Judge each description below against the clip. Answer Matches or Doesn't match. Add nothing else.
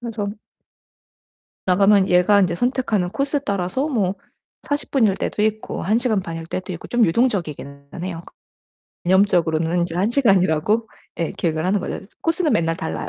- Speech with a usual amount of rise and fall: Matches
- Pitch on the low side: Doesn't match